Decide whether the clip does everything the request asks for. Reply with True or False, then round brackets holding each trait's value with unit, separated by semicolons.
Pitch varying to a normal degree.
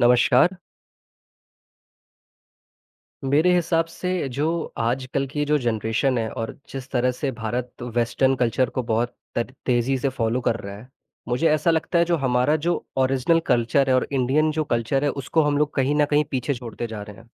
True (3.5 semitones)